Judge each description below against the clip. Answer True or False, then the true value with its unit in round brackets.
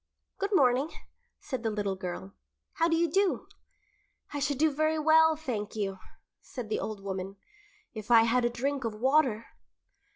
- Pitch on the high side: True (250 Hz)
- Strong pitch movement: True (6.5 semitones)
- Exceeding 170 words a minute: False (165 wpm)